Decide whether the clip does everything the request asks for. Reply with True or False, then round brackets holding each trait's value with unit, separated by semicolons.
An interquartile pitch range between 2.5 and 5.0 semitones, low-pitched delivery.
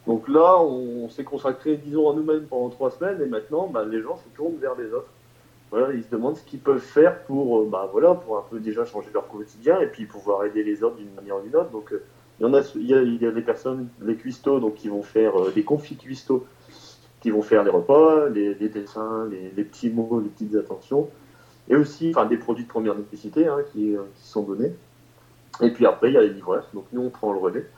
False (5.5 semitones; 120 Hz)